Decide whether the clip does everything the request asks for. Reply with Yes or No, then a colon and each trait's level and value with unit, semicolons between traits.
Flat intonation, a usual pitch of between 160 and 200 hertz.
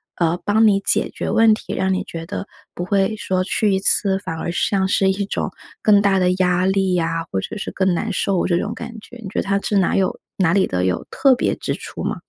Yes: narrow, 2.2 semitones; high, 190 Hz